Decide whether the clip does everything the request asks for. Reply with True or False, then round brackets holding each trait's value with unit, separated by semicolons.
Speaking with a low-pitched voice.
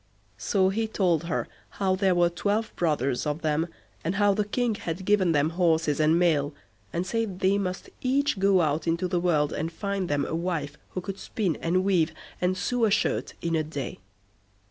False (180 Hz)